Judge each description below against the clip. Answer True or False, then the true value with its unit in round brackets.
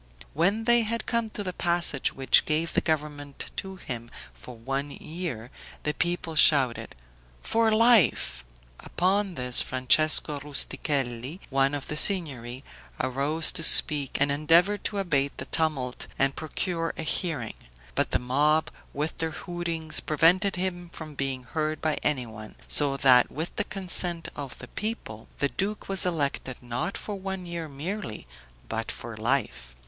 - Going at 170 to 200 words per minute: False (150 wpm)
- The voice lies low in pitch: False (155 Hz)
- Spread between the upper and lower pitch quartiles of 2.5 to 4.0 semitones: False (4.7 semitones)